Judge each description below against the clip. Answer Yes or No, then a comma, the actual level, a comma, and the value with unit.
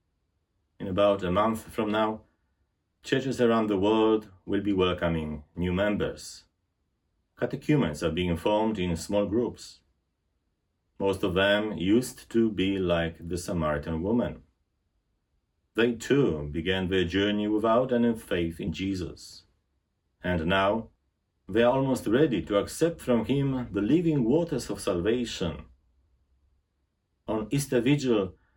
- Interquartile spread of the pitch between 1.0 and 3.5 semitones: No, average, 4.8 semitones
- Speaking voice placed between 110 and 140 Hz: No, very low, 95 Hz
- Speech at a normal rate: No, slow, 125 wpm